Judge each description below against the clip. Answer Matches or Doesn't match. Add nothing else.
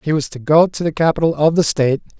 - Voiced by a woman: Doesn't match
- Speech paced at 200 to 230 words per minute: Doesn't match